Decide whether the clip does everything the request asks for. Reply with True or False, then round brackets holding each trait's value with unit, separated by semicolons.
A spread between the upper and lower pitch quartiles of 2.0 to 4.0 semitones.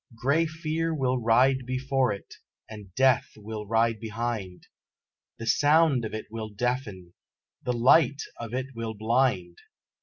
True (3.4 semitones)